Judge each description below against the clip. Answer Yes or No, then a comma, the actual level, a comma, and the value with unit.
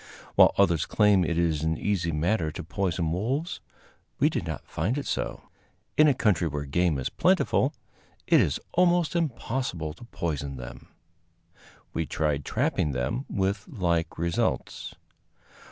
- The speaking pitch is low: Yes, very low, 85 Hz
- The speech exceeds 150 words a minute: No, average, 145 wpm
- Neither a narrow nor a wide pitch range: No, wide, 5.8 semitones